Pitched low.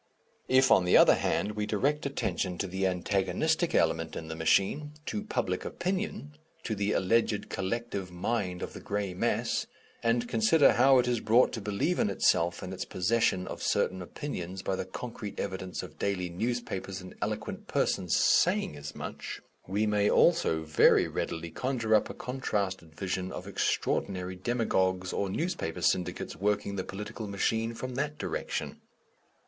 Yes: low, 100 Hz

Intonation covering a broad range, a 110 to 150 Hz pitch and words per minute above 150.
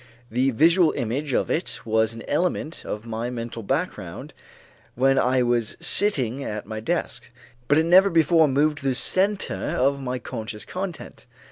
Yes: wide, 5.7 semitones; low, 135 Hz; average, 160 wpm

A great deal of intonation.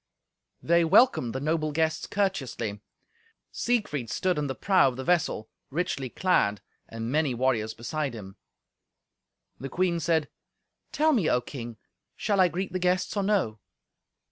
Yes: wide, 6.9 semitones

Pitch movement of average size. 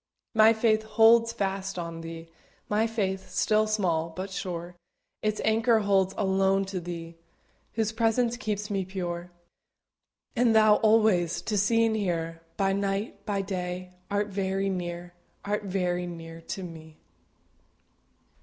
Yes: average, 3.4 semitones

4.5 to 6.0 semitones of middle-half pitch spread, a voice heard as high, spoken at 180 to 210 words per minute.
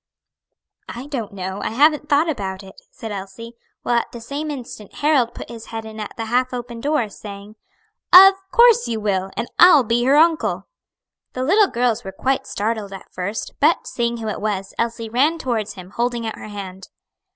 Yes: average, 5.0 semitones; high, 235 Hz; average, 195 wpm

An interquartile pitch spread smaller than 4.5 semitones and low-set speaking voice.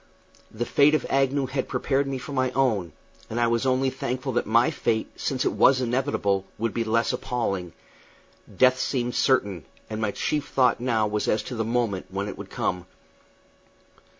Yes: average, 3.3 semitones; low, 120 Hz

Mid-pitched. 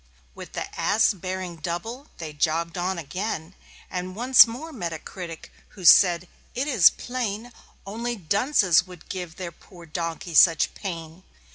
Yes: medium, 180 Hz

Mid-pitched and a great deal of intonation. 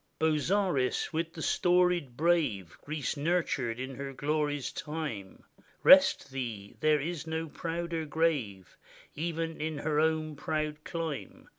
No: medium, 155 Hz; average, 3.1 semitones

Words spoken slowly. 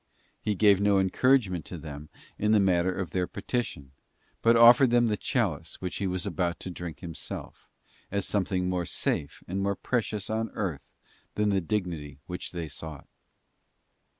No: average, 165 wpm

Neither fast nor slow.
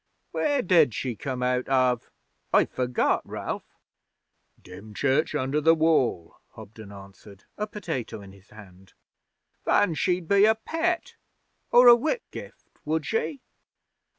No: slow, 125 wpm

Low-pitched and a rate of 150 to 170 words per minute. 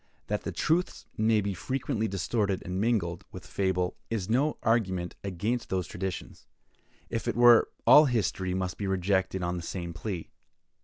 Yes: very low, 95 Hz; average, 160 wpm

